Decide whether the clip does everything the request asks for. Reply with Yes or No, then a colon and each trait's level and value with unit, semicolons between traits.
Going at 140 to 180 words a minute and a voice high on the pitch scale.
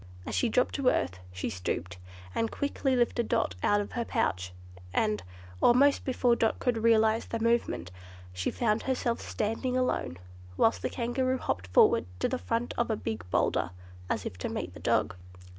Yes: average, 175 wpm; high, 230 Hz